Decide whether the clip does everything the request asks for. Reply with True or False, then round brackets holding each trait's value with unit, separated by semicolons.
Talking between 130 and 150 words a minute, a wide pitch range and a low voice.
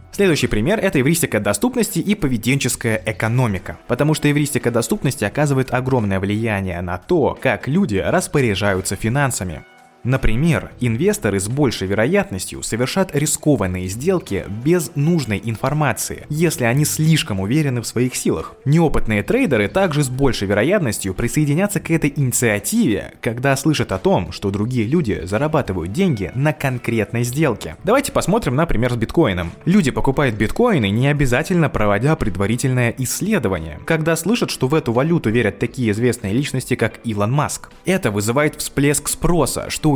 True (140 wpm; 6.0 semitones; 125 Hz)